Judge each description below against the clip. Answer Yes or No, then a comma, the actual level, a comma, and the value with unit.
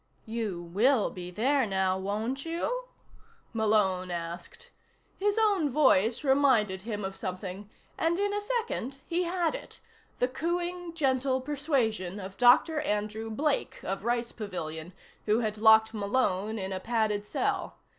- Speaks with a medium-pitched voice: No, high, 225 Hz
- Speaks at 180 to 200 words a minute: No, average, 140 wpm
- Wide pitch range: Yes, wide, 6.6 semitones